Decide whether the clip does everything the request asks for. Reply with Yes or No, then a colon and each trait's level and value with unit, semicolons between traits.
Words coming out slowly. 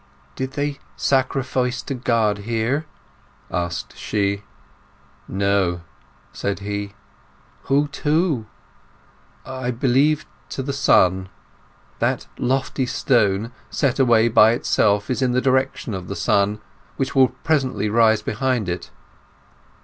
Yes: slow, 115 wpm